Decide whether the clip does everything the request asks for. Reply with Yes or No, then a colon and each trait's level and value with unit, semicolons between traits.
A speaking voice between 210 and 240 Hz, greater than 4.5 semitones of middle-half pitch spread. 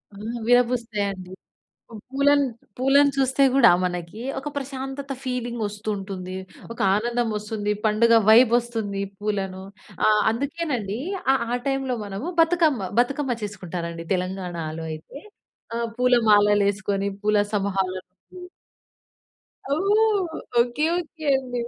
Yes: high, 230 Hz; average, 5.2 semitones